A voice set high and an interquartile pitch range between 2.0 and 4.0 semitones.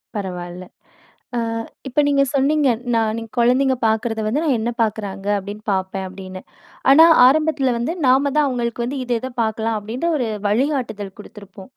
No: high, 230 Hz; average, 4.6 semitones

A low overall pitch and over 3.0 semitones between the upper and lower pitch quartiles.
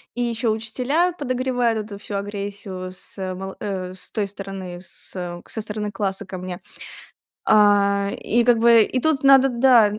No: high, 210 Hz; average, 3.7 semitones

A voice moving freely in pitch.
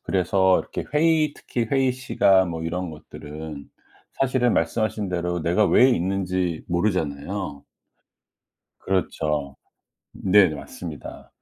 No: average, 4.9 semitones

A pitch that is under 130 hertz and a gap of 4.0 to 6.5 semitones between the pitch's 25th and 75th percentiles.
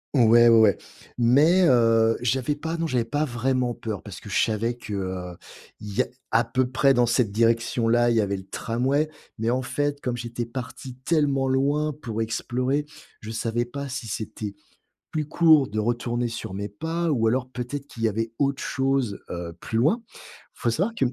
No: low, 120 Hz; average, 3.4 semitones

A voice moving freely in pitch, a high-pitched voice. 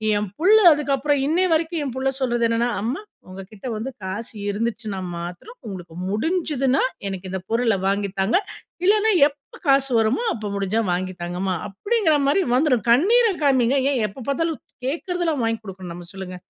Yes: wide, 7.2 semitones; high, 240 Hz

